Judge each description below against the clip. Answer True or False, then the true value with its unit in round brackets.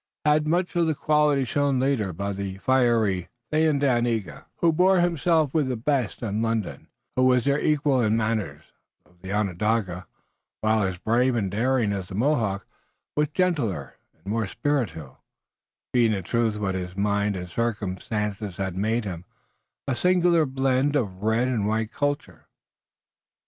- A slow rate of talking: False (160 wpm)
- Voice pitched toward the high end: False (115 Hz)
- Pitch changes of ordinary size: False (6.0 semitones)